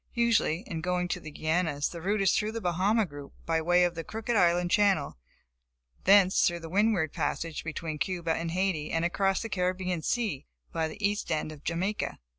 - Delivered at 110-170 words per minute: No, average, 195 wpm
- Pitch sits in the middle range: Yes, medium, 175 Hz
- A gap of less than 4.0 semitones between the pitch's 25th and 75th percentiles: Yes, average, 3.5 semitones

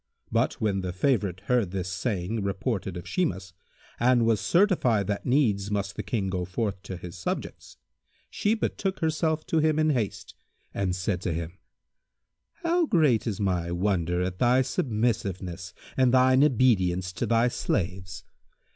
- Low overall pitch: Yes, low, 100 Hz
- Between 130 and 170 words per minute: Yes, average, 155 wpm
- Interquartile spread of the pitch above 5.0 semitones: Yes, wide, 5.6 semitones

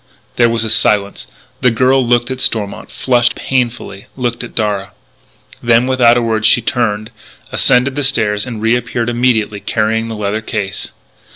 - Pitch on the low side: Yes, low, 115 Hz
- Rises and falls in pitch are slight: Yes, narrow, 2.3 semitones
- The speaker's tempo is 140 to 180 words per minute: Yes, average, 160 wpm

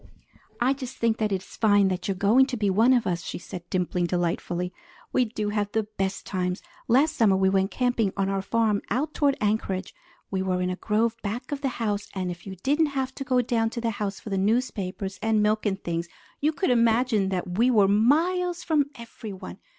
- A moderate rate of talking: No, fast, 220 wpm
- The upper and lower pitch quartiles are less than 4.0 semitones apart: No, average, 4.3 semitones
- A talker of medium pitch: No, high, 215 Hz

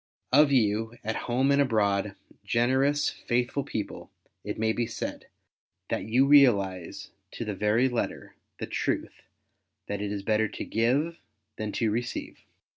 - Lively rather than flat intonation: No, average, 3.8 semitones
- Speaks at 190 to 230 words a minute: No, average, 145 wpm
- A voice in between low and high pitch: No, low, 115 Hz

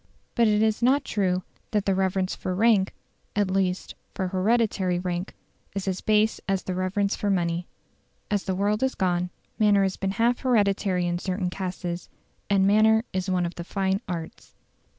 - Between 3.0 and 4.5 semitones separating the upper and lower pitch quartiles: No, narrow, 2.5 semitones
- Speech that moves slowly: No, average, 175 wpm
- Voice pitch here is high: Yes, high, 195 Hz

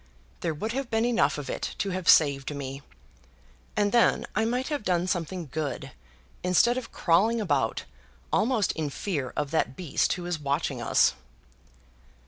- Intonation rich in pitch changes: Yes, wide, 7.0 semitones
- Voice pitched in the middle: Yes, medium, 180 Hz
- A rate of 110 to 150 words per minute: No, average, 160 wpm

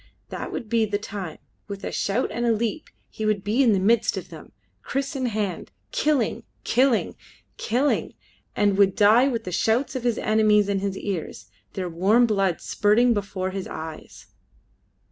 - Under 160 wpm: No, average, 175 wpm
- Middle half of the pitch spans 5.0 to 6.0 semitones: No, average, 3.3 semitones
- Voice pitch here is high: Yes, high, 210 Hz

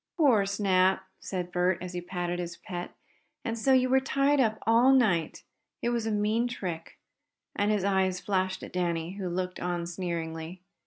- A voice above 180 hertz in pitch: Yes, high, 190 Hz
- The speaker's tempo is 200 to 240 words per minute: No, average, 175 wpm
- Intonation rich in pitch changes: No, average, 4.0 semitones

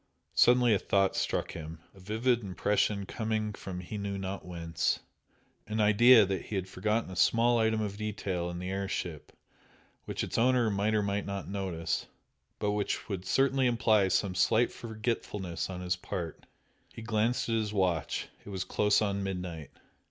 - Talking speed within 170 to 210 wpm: Yes, average, 175 wpm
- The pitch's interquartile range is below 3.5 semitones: Yes, average, 2.9 semitones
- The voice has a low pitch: Yes, low, 100 Hz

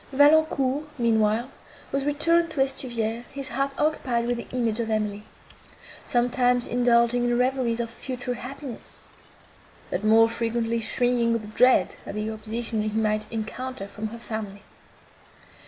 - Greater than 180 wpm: No, average, 140 wpm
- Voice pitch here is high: Yes, high, 235 Hz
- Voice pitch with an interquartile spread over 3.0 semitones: No, average, 2.7 semitones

